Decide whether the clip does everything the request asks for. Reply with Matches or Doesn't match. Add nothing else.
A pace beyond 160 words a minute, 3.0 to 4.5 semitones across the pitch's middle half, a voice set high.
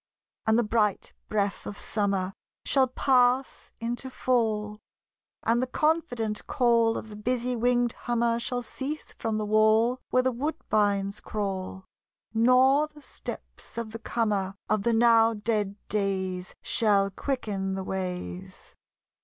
Doesn't match